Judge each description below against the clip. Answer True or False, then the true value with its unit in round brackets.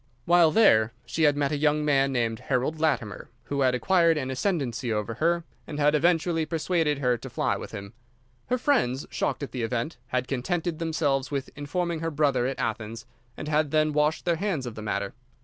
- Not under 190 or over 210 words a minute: True (200 wpm)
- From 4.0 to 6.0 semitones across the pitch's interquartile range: True (4.4 semitones)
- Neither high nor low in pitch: True (145 Hz)